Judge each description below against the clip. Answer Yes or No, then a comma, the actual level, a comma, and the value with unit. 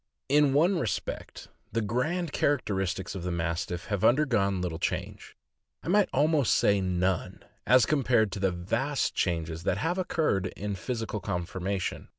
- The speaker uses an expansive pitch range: Yes, wide, 7.6 semitones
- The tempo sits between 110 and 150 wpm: No, average, 160 wpm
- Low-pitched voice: Yes, low, 105 Hz